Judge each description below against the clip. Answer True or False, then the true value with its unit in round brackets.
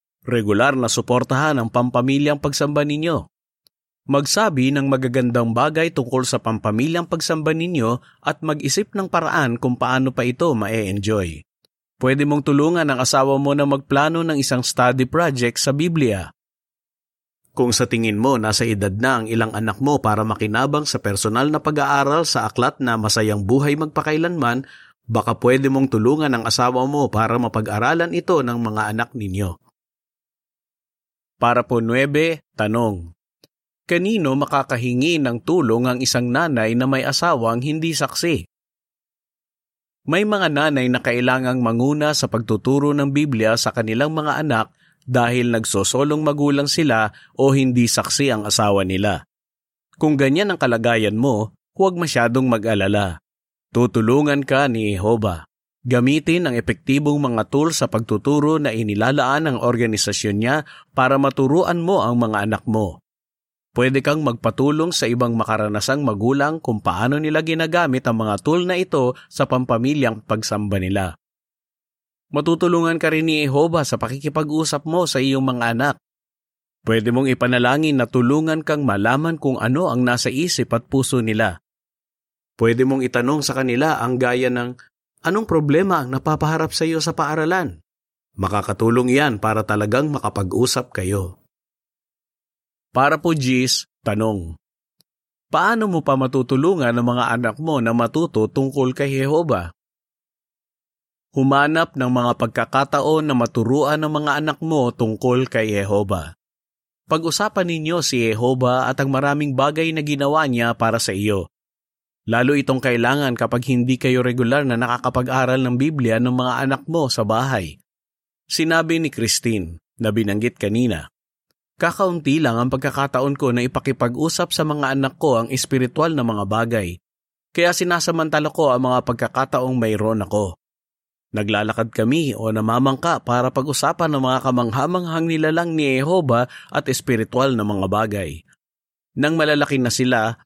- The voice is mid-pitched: False (130 Hz)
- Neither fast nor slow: True (140 wpm)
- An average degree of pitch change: True (4.2 semitones)